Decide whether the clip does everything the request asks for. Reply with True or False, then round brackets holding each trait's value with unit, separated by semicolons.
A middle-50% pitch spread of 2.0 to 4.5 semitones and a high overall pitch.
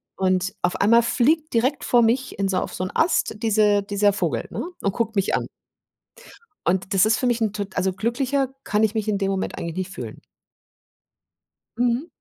True (3.6 semitones; 210 Hz)